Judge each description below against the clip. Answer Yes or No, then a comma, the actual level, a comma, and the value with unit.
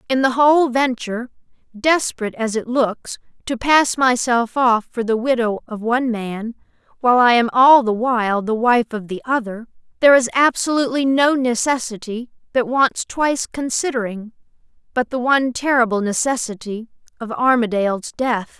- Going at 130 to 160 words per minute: Yes, average, 140 wpm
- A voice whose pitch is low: No, high, 240 Hz